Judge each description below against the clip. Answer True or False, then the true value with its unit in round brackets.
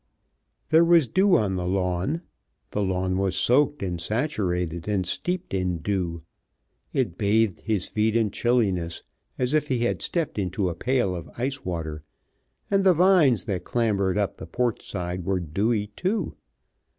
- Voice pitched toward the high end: False (105 Hz)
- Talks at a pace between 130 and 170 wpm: True (160 wpm)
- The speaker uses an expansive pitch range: True (5.9 semitones)